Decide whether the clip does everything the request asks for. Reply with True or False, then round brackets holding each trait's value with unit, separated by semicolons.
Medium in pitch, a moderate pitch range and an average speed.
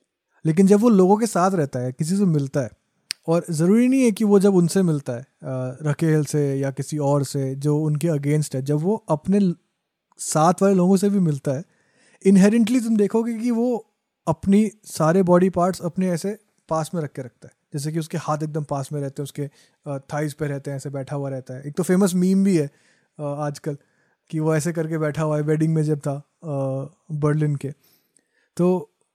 False (160 Hz; 4.7 semitones; 205 wpm)